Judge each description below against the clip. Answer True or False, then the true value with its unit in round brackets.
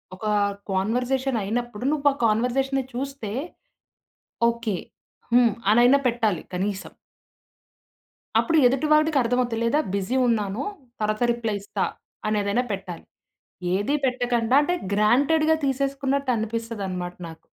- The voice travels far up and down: False (4.2 semitones)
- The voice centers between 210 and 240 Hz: True (235 Hz)